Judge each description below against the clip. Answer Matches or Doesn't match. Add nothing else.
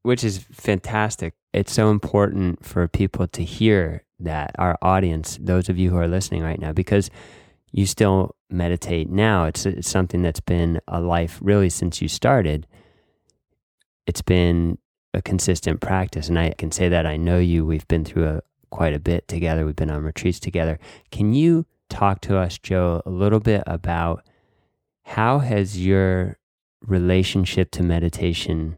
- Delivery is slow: Doesn't match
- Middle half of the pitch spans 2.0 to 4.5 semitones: Matches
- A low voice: Matches